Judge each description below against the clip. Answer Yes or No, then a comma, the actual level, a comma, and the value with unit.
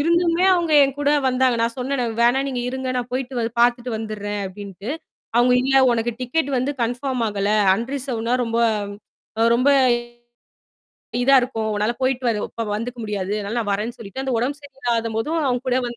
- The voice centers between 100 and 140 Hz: No, high, 245 Hz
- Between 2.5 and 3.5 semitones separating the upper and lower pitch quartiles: Yes, average, 2.8 semitones